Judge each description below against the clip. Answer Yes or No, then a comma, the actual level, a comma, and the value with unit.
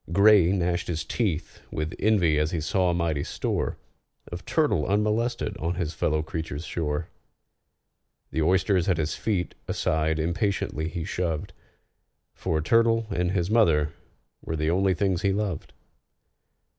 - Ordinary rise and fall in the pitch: Yes, average, 3.8 semitones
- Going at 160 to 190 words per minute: No, average, 145 wpm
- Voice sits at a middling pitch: No, very low, 85 Hz